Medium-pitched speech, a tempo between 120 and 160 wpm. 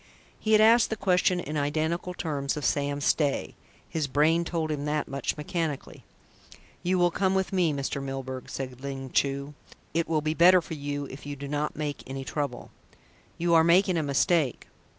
No: medium, 150 Hz; average, 185 wpm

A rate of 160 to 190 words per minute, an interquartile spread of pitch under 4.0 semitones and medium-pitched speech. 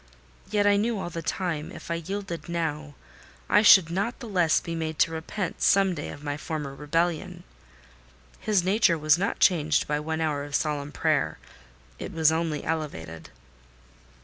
Yes: average, 170 wpm; average, 3.6 semitones; medium, 165 Hz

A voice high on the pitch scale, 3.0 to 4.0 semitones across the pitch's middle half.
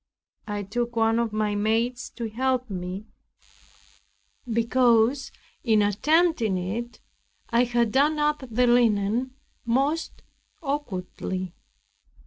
Yes: high, 235 Hz; average, 3.3 semitones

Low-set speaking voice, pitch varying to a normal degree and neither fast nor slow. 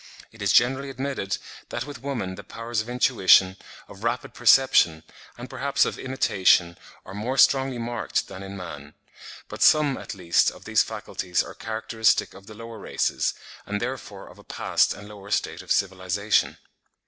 Yes: low, 110 Hz; average, 4.5 semitones; average, 170 wpm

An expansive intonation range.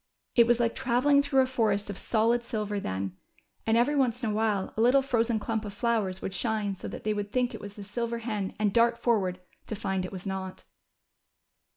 No: average, 2.9 semitones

